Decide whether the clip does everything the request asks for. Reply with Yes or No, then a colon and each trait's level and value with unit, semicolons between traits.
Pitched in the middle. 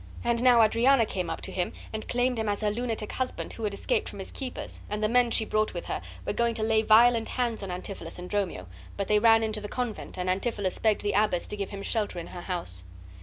No: high, 215 Hz